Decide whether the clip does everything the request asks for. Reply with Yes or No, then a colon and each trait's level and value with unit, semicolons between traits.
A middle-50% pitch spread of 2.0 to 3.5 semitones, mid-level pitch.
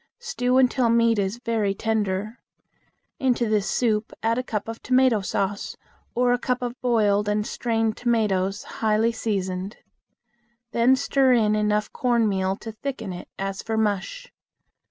No: average, 2.9 semitones; high, 225 Hz